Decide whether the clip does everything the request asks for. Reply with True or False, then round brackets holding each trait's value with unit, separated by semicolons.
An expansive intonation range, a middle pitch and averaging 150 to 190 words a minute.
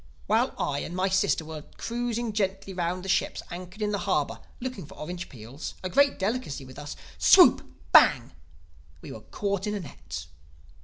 True (6.8 semitones; 180 Hz; 165 wpm)